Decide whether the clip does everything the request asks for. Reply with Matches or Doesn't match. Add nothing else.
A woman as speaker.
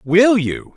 Doesn't match